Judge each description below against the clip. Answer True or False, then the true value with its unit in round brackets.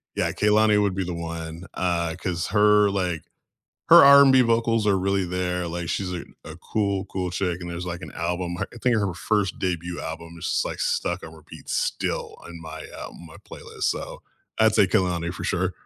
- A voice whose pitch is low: True (90 Hz)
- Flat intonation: False (3.2 semitones)